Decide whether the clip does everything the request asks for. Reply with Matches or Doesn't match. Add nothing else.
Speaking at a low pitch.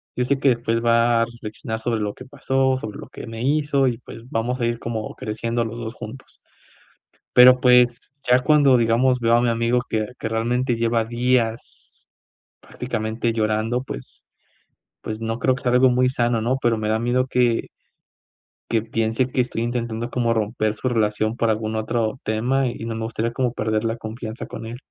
Matches